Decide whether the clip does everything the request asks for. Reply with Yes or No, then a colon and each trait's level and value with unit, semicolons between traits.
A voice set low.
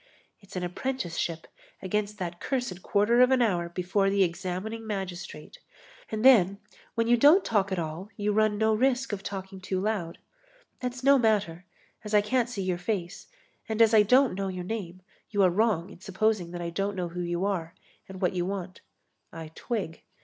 No: high, 195 Hz